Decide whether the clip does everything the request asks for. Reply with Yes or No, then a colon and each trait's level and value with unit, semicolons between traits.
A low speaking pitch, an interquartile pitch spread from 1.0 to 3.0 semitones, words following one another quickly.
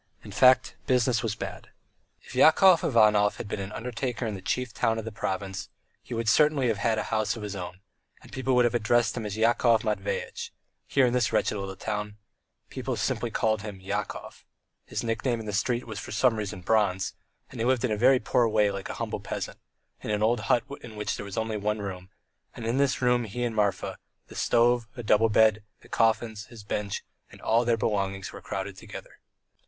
Yes: low, 110 Hz; narrow, 2.6 semitones; fast, 210 wpm